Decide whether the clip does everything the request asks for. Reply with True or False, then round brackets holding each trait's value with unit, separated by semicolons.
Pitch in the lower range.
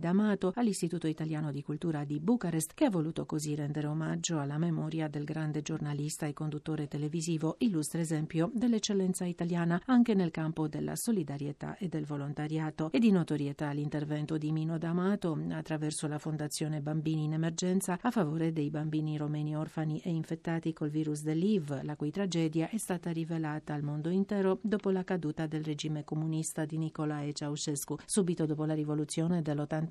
False (155 Hz)